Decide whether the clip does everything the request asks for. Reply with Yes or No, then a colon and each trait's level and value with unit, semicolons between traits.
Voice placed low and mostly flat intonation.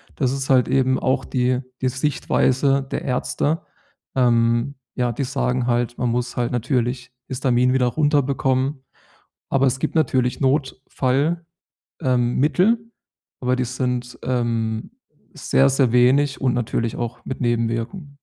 Yes: low, 130 Hz; narrow, 1.9 semitones